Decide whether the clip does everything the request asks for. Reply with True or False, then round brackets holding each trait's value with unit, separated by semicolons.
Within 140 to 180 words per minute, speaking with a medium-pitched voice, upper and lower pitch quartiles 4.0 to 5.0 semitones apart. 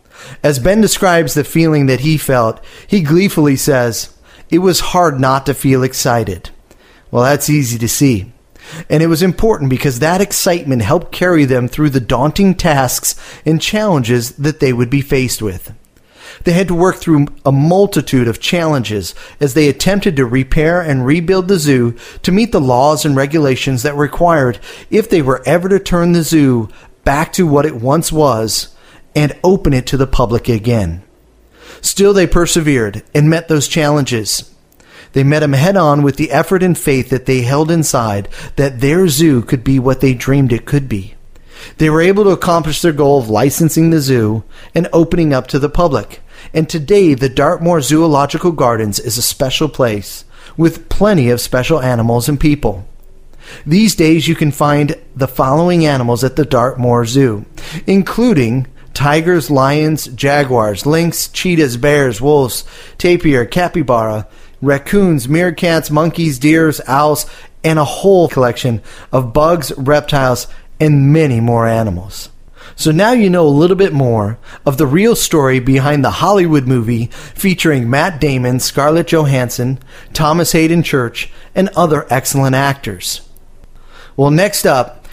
True (160 wpm; 145 Hz; 4.6 semitones)